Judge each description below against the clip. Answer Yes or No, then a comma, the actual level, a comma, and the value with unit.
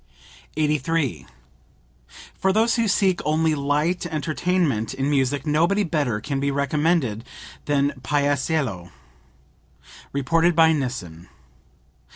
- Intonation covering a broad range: No, average, 3.3 semitones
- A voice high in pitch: No, medium, 150 Hz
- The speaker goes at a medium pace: No, slow, 100 wpm